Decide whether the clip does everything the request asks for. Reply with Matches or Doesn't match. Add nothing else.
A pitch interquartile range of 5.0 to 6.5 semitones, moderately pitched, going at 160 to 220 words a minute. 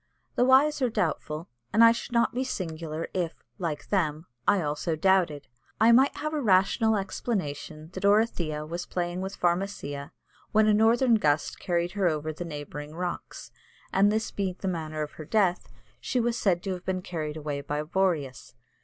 Matches